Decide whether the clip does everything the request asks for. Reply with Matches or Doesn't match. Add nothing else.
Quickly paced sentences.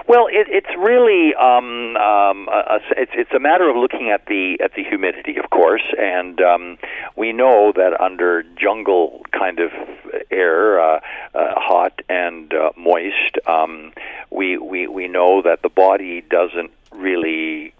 Doesn't match